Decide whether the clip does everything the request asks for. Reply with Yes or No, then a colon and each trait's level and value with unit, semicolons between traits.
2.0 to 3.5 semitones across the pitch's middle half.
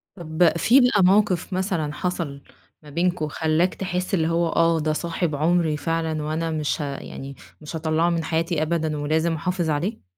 Yes: narrow, 2.4 semitones